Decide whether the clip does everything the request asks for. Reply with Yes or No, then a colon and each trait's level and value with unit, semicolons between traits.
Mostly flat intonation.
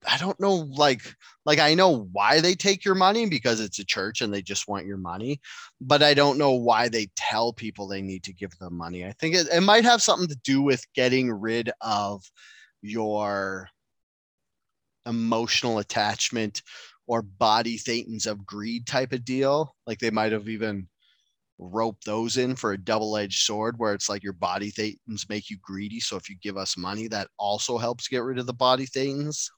No: average, 4.7 semitones